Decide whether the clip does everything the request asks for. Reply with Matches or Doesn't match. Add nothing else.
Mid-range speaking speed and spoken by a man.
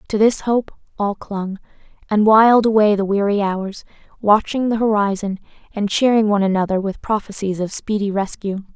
Doesn't match